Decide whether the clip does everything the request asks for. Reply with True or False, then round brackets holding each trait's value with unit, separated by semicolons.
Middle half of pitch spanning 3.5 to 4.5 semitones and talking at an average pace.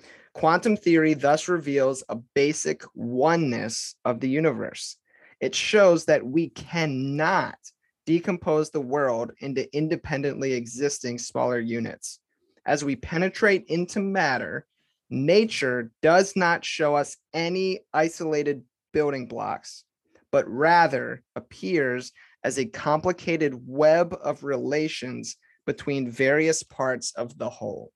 False (3.8 semitones; 110 wpm)